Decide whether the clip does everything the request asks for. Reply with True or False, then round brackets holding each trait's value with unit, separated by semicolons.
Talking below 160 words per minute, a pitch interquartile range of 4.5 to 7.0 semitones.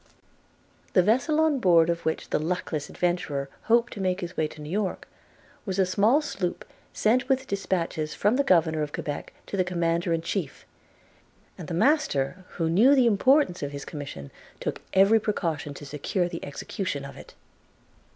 False (175 wpm; 5.2 semitones)